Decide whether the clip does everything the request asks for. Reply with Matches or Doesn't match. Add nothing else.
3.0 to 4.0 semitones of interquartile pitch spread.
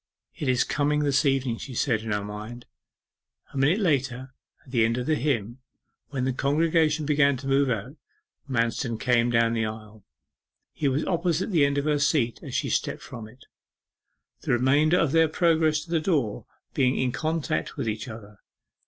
Doesn't match